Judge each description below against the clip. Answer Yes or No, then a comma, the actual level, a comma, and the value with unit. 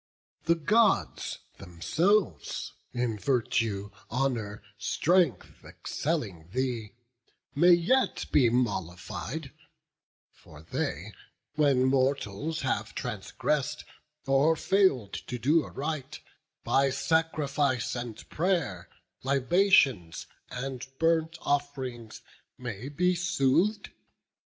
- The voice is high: No, low, 135 Hz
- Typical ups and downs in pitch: No, wide, 5.8 semitones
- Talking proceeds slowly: Yes, slow, 85 wpm